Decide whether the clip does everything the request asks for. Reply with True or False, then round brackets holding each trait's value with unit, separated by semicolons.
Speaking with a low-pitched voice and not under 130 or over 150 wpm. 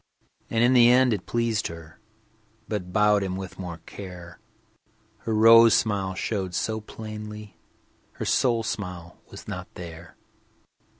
True (105 Hz; 135 wpm)